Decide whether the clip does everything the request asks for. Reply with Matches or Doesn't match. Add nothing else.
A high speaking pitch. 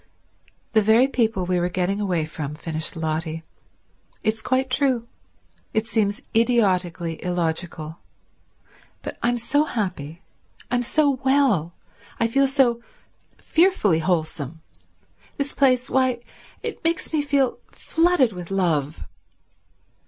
Matches